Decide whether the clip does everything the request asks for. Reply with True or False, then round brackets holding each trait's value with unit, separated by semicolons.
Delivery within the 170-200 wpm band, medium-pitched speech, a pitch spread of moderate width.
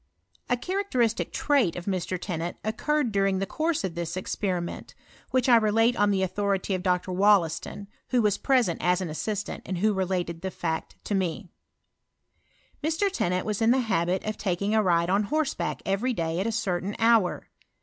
False (180 wpm; 200 Hz; 4.1 semitones)